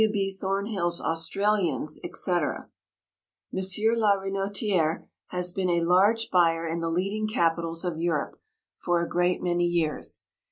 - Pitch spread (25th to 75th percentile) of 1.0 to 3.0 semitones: Yes, average, 2.7 semitones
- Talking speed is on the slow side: Yes, slow, 125 wpm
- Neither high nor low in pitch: Yes, medium, 175 Hz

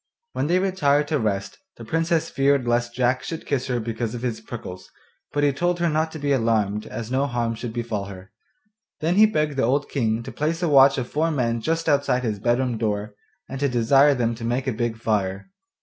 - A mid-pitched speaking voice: No, low, 125 Hz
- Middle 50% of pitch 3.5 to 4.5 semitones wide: Yes, average, 4.2 semitones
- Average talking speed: No, fast, 220 wpm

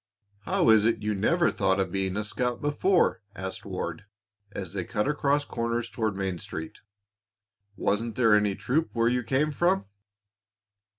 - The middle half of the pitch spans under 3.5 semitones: No, average, 4.9 semitones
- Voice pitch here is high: No, low, 115 Hz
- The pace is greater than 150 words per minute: Yes, average, 160 wpm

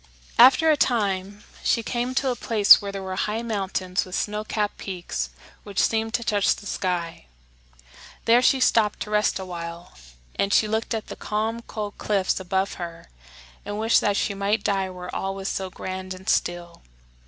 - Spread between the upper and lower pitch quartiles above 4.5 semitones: No, average, 2.8 semitones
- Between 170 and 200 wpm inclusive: Yes, average, 190 wpm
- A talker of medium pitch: No, high, 200 Hz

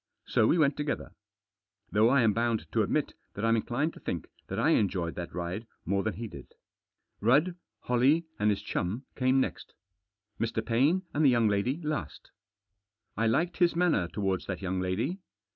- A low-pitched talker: Yes, low, 115 Hz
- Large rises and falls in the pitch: Yes, wide, 6.1 semitones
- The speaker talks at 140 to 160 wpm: No, average, 175 wpm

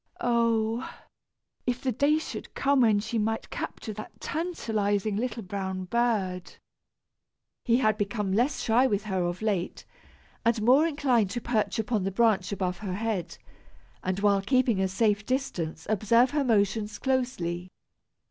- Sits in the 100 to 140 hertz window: No, high, 215 Hz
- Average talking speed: Yes, average, 145 wpm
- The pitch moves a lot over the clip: No, average, 3.6 semitones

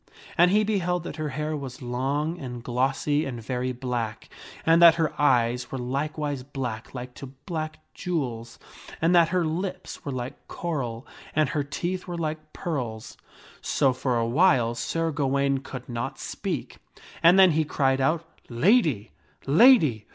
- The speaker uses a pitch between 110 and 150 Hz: Yes, medium, 140 Hz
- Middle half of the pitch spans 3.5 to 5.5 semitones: Yes, average, 4.7 semitones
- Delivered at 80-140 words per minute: No, average, 160 wpm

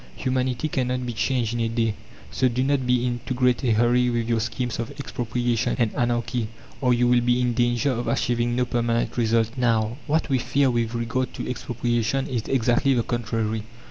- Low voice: Yes, low, 120 Hz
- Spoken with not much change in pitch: Yes, narrow, 1.4 semitones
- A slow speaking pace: No, average, 200 wpm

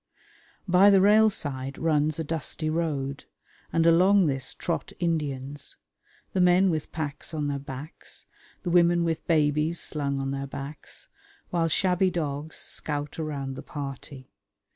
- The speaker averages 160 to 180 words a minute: No, average, 140 wpm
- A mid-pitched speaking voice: Yes, medium, 155 Hz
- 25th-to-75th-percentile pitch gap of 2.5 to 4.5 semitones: Yes, average, 3.4 semitones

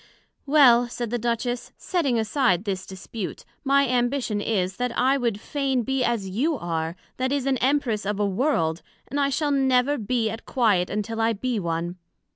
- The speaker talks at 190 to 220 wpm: No, average, 180 wpm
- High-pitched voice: Yes, high, 240 Hz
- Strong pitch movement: No, average, 4.5 semitones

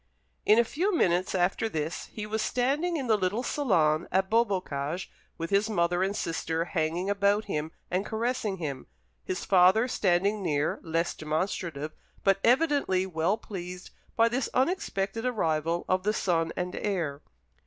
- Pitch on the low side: No, high, 190 Hz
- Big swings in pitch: No, average, 4.6 semitones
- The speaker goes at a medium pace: Yes, average, 155 wpm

